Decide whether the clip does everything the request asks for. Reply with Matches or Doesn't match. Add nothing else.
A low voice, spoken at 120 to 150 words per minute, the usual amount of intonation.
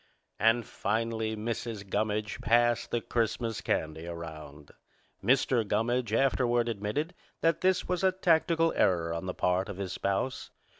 Matches